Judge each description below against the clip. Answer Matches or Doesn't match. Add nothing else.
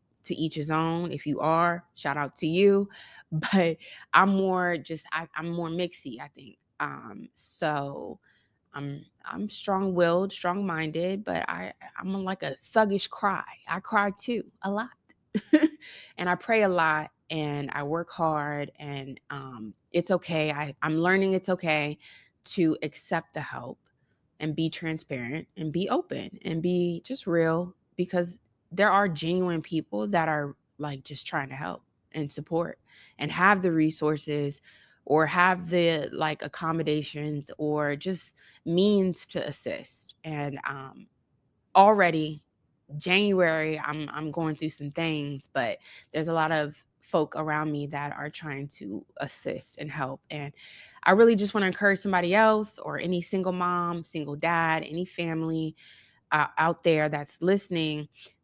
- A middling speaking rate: Matches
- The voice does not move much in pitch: Doesn't match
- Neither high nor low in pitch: Matches